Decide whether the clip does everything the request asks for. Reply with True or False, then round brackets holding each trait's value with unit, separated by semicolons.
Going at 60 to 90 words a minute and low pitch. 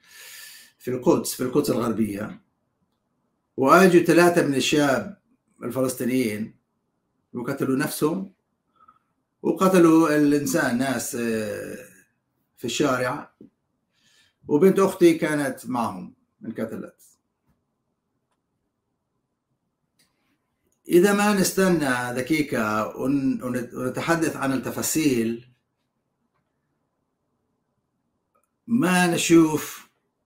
False (65 wpm; 150 Hz)